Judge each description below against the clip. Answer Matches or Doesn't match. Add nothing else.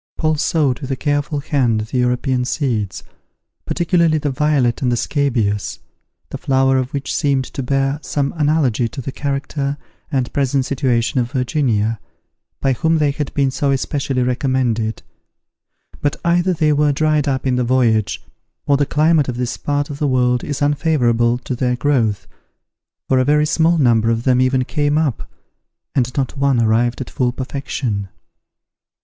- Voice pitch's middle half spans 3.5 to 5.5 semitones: Doesn't match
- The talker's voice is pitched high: Doesn't match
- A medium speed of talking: Matches